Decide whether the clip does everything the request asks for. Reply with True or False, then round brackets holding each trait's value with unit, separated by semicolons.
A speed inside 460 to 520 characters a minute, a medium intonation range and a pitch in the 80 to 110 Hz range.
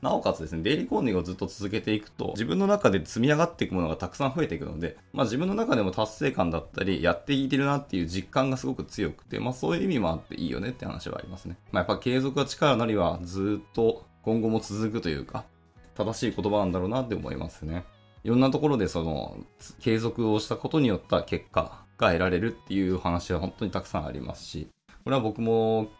True (480 characters per minute; 4.8 semitones; 105 Hz)